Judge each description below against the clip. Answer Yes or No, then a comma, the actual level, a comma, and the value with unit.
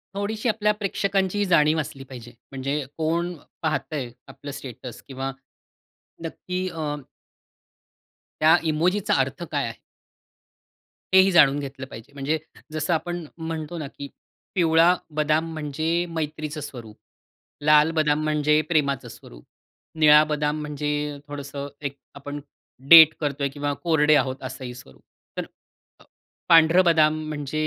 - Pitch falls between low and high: Yes, medium, 150 Hz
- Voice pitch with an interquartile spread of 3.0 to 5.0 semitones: No, narrow, 2.5 semitones